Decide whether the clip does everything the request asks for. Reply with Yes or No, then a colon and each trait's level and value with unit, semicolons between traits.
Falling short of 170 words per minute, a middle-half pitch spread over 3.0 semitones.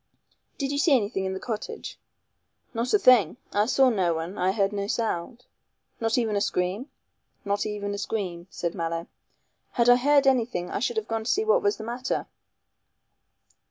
No: average, 185 wpm; average, 4.4 semitones